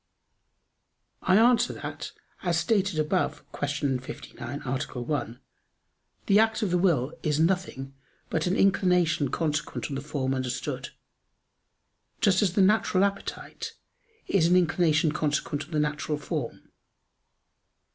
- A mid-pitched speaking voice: Yes, medium, 160 Hz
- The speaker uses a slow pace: Yes, slow, 125 wpm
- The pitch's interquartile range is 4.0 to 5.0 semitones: Yes, average, 4.7 semitones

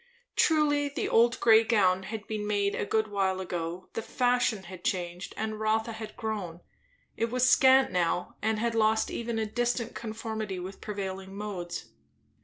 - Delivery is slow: No, average, 165 wpm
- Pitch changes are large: No, average, 3.1 semitones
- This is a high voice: Yes, high, 215 Hz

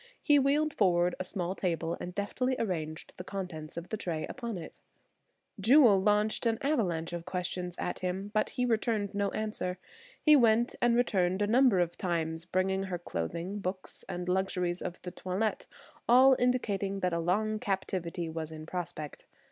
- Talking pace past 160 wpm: Yes, average, 170 wpm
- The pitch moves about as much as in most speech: Yes, average, 3.8 semitones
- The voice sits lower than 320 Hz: Yes, high, 190 Hz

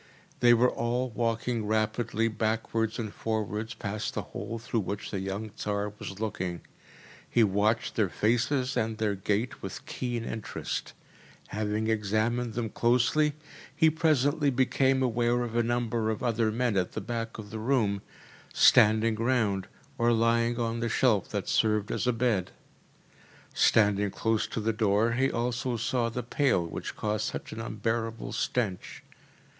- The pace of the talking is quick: No, average, 155 wpm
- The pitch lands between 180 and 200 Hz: No, low, 115 Hz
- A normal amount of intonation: No, narrow, 2.1 semitones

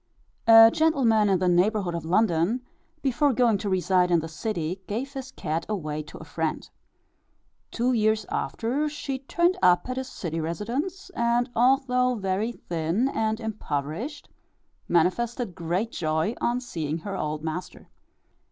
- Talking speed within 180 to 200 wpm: No, average, 145 wpm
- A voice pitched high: Yes, high, 215 Hz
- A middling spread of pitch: No, wide, 6.5 semitones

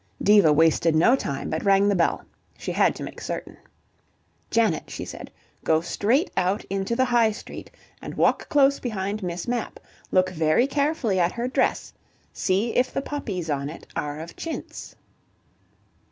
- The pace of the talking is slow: No, average, 165 wpm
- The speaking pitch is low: No, high, 200 Hz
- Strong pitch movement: Yes, wide, 6.2 semitones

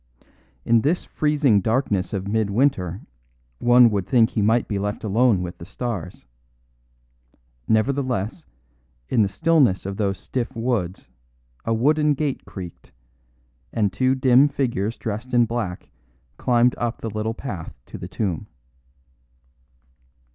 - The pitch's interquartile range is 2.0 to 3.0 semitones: No, average, 4.3 semitones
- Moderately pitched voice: No, low, 115 Hz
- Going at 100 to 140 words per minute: Yes, slow, 135 wpm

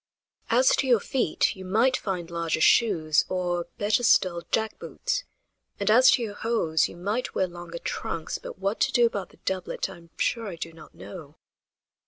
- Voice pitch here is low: No, high, 190 Hz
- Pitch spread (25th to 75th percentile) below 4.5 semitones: No, average, 4.9 semitones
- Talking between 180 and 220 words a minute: Yes, average, 190 wpm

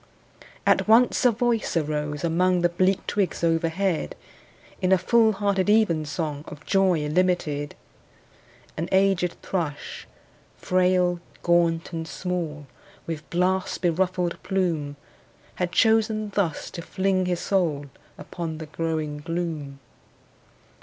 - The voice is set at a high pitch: No, medium, 175 Hz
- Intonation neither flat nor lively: Yes, average, 3.1 semitones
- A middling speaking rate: No, slow, 115 wpm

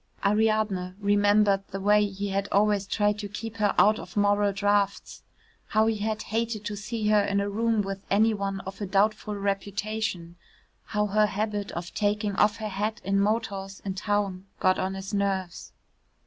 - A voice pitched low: No, high, 205 Hz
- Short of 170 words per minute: No, average, 175 wpm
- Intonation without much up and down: Yes, narrow, 1.4 semitones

